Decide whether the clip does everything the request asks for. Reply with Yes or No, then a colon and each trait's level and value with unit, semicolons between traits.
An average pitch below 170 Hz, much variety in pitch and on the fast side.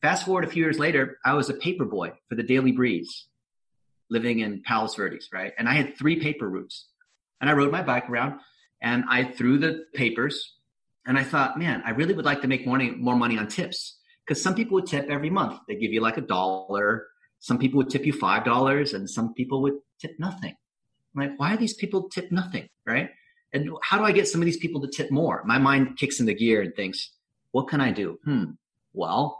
Yes: medium, 140 Hz; wide, 5.7 semitones; fast, 225 wpm